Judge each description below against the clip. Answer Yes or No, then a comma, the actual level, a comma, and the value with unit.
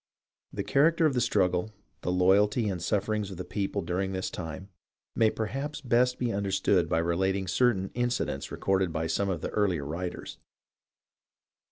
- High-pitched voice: No, very low, 95 Hz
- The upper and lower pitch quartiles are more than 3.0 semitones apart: Yes, average, 3.8 semitones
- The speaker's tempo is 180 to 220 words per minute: No, average, 160 wpm